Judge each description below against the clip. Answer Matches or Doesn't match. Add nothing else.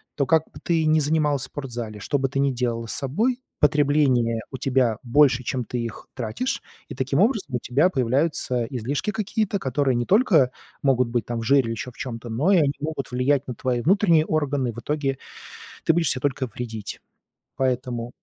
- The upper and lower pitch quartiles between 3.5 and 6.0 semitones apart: Matches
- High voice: Doesn't match